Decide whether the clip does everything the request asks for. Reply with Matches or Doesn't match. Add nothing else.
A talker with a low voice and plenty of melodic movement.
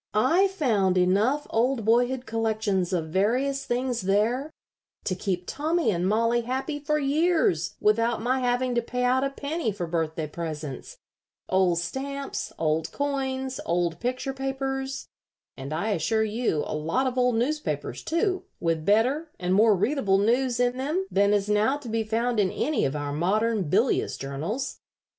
Doesn't match